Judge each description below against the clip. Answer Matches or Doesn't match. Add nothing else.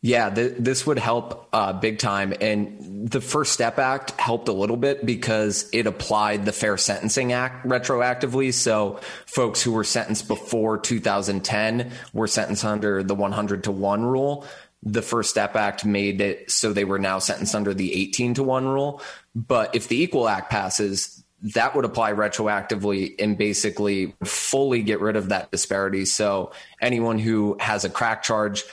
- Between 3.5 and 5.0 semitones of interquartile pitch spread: Doesn't match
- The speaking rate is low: Doesn't match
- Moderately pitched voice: Doesn't match